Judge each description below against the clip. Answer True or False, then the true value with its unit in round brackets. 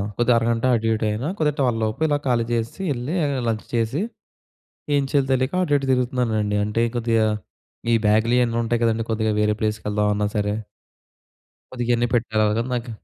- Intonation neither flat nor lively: False (2.3 semitones)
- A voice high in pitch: False (115 Hz)